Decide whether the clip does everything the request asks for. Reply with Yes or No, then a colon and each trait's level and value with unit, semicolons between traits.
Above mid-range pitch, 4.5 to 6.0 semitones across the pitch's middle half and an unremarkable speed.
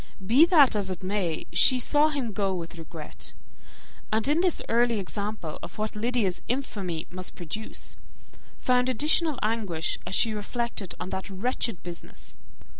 Yes: high, 215 Hz; average, 5.2 semitones; average, 150 wpm